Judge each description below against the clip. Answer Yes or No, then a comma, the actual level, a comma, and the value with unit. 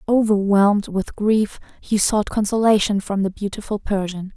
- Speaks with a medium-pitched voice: No, high, 205 Hz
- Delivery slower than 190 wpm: Yes, average, 140 wpm